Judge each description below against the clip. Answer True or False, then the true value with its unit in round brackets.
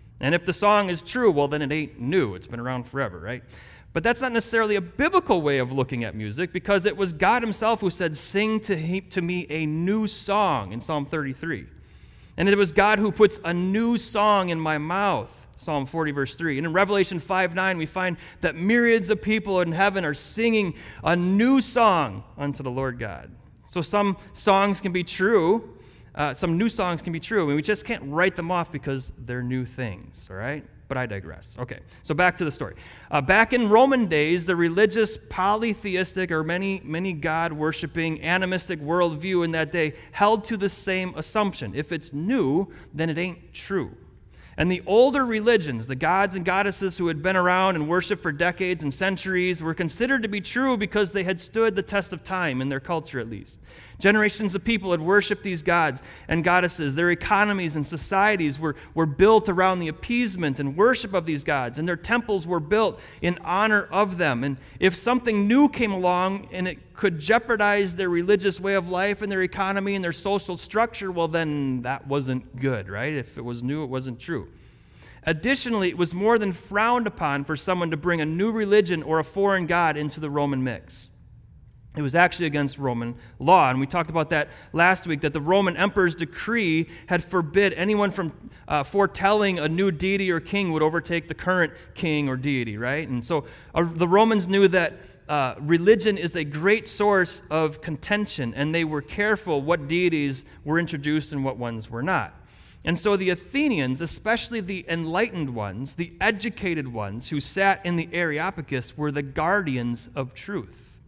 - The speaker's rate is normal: True (195 wpm)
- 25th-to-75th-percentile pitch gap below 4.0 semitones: False (5.1 semitones)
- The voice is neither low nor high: True (175 Hz)